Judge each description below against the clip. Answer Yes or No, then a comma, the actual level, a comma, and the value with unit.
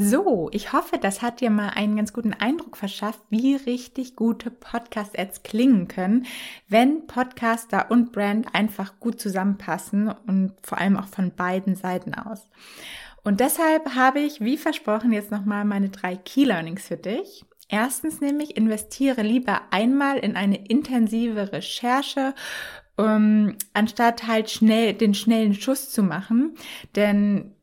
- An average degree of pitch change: Yes, average, 3.6 semitones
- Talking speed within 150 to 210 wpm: No, average, 140 wpm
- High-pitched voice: Yes, high, 220 Hz